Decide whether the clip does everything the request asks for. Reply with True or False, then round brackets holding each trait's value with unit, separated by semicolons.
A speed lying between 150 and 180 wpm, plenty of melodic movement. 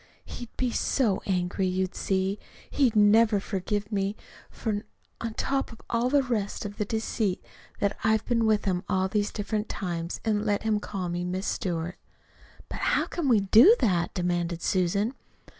False (170 wpm; 2.9 semitones)